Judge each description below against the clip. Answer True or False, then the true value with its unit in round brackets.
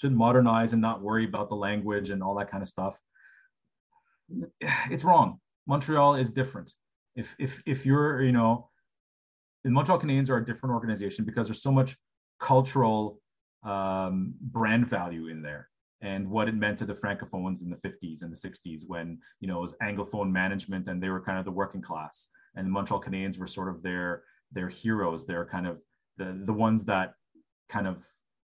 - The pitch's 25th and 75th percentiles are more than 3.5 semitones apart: True (4.0 semitones)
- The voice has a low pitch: True (100 Hz)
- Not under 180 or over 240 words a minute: True (185 wpm)